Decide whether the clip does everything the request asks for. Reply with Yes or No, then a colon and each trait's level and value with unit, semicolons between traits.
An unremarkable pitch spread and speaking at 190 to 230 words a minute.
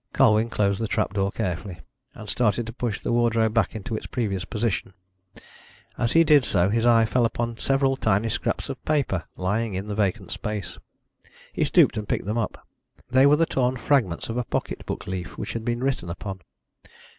Yes: average, 3.5 semitones; average, 195 wpm